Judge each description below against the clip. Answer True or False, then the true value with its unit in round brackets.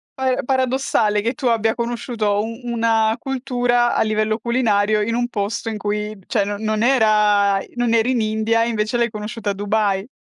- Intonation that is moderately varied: False (2.3 semitones)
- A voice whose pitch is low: False (220 Hz)